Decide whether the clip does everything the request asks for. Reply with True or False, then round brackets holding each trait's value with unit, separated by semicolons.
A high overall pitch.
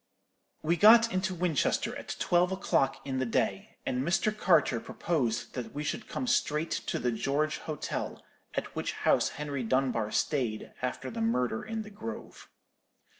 False (150 Hz)